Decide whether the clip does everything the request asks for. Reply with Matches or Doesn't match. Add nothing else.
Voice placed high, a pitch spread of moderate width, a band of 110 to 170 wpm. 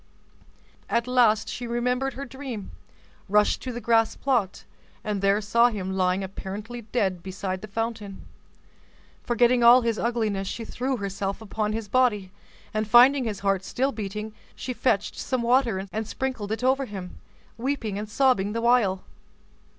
Matches